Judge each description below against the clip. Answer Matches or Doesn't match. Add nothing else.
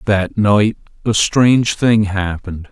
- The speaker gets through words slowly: Matches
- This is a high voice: Doesn't match